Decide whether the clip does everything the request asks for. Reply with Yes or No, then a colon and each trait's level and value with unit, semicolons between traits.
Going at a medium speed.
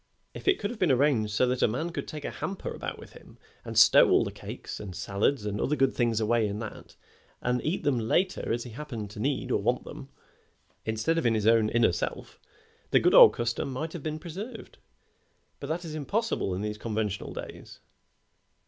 No: fast, 210 wpm